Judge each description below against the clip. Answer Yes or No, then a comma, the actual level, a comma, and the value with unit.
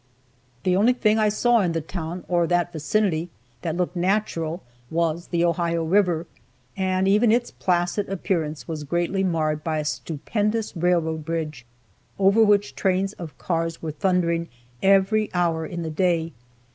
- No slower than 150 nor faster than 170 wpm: Yes, average, 155 wpm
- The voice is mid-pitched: Yes, medium, 175 Hz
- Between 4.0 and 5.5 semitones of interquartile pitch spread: No, average, 3.1 semitones